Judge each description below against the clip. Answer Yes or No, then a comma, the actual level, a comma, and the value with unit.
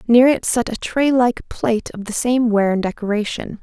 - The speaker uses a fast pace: Yes, fast, 215 wpm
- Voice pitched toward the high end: Yes, high, 225 Hz